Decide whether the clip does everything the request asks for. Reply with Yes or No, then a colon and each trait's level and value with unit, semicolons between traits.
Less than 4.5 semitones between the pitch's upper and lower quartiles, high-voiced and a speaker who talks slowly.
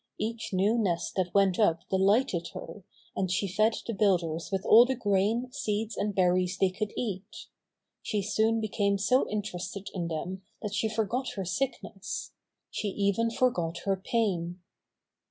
No: average, 3.1 semitones; high, 200 Hz; average, 155 wpm